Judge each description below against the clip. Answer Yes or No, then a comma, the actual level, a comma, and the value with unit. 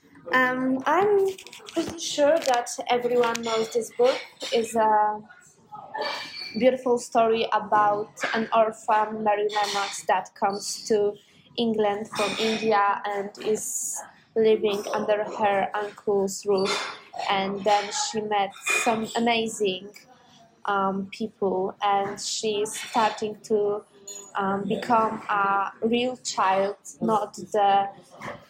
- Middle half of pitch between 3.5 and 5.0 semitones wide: No, narrow, 2.4 semitones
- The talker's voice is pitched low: No, high, 215 Hz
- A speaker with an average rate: No, slow, 105 wpm